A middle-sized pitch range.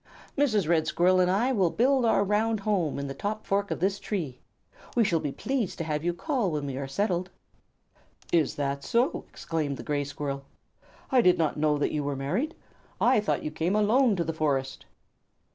No: wide, 6.3 semitones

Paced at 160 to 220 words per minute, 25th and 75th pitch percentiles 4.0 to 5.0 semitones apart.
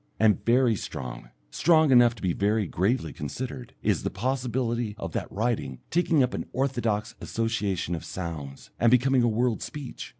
Yes: average, 165 wpm; average, 4.3 semitones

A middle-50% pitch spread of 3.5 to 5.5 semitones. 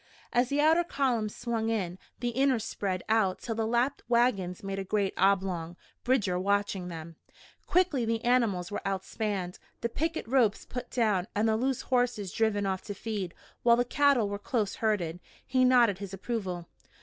Yes: average, 4.1 semitones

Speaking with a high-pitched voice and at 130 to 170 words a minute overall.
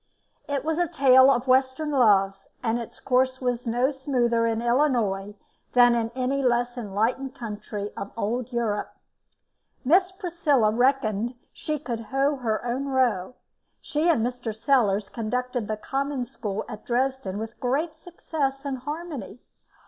Yes: very high, 250 Hz; average, 145 wpm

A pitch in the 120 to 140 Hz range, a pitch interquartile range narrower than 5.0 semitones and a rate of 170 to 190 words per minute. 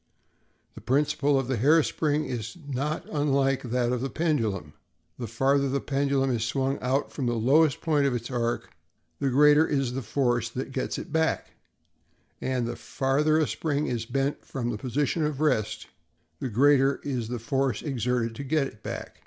Yes: low, 135 Hz; average, 3.1 semitones; average, 180 wpm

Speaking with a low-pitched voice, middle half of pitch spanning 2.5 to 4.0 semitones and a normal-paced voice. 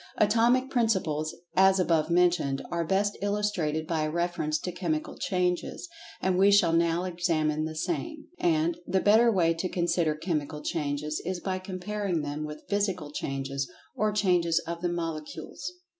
No: medium, 175 Hz; average, 3.6 semitones; average, 155 wpm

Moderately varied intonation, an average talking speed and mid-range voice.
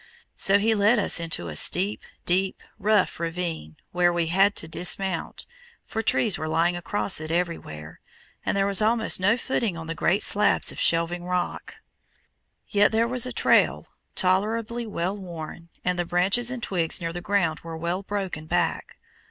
Yes: average, 3.5 semitones; average, 170 wpm; medium, 180 Hz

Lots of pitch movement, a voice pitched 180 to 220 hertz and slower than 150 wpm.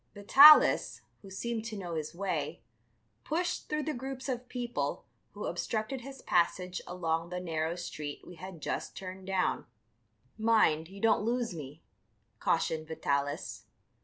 Yes: wide, 6.4 semitones; high, 190 Hz; average, 140 wpm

